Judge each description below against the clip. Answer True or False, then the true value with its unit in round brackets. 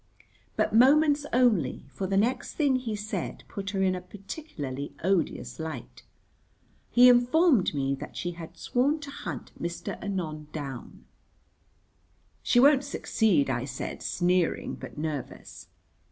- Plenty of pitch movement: True (7.9 semitones)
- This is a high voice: True (195 Hz)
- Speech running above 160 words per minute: False (135 wpm)